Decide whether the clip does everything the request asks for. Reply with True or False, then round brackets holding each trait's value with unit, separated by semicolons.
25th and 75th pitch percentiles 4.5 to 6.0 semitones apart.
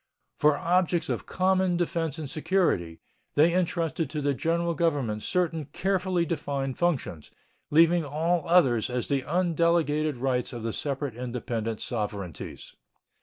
True (5.1 semitones)